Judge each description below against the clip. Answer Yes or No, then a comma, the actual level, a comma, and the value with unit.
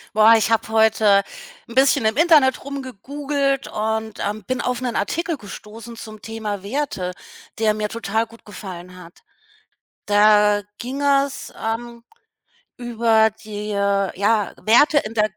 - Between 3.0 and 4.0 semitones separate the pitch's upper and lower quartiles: Yes, average, 3.5 semitones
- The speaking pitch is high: Yes, high, 220 Hz